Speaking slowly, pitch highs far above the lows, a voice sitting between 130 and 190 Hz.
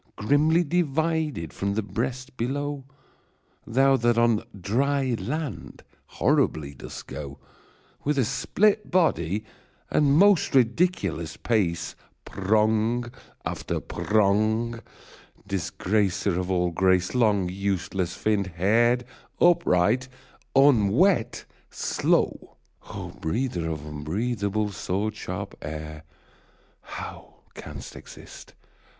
No: slow, 95 wpm; wide, 6.3 semitones; low, 110 Hz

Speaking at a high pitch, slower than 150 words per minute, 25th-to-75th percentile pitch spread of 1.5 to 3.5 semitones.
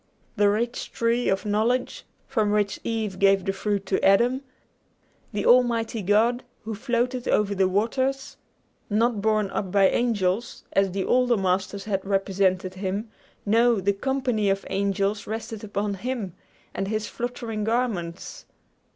Yes: high, 210 Hz; average, 140 wpm; average, 3.2 semitones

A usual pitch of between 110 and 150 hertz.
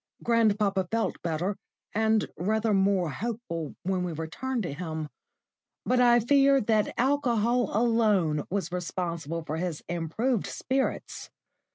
No: high, 205 Hz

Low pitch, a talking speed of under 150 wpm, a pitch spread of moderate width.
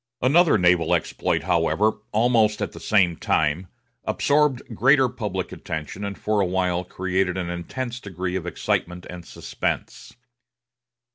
Yes: very low, 95 Hz; slow, 135 wpm; average, 4.5 semitones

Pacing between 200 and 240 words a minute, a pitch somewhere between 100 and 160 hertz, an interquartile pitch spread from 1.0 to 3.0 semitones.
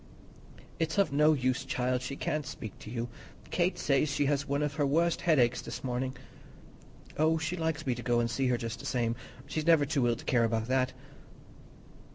No: fast, 205 wpm; low, 135 Hz; average, 3.8 semitones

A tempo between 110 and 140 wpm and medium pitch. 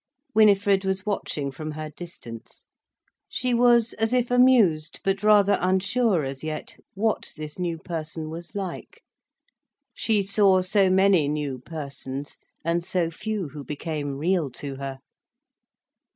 Yes: slow, 135 wpm; medium, 175 Hz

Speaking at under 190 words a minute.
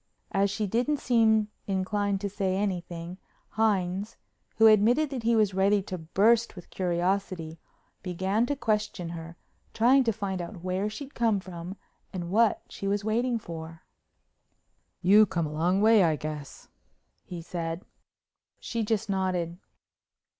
Yes: average, 145 wpm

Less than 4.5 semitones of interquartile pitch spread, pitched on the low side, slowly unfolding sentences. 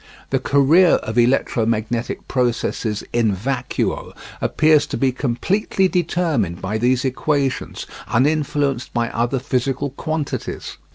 Yes: average, 3.8 semitones; low, 130 Hz; slow, 110 wpm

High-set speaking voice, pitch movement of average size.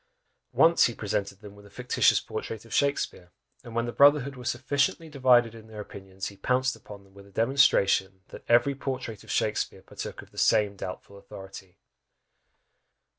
No: low, 115 Hz; average, 4.6 semitones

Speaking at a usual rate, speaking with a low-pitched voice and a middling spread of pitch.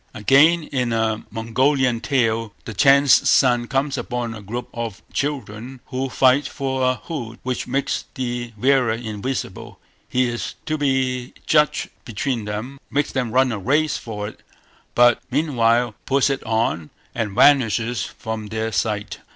Yes: average, 150 wpm; low, 125 Hz; average, 3.2 semitones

